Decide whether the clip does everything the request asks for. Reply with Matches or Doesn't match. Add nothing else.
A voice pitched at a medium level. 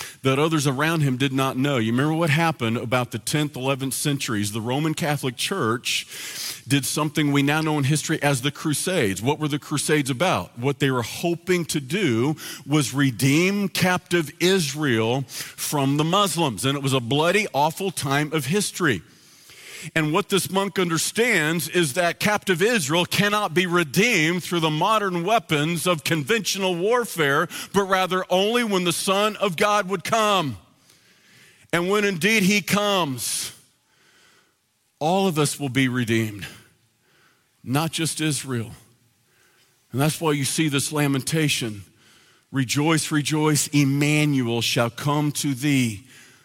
Matches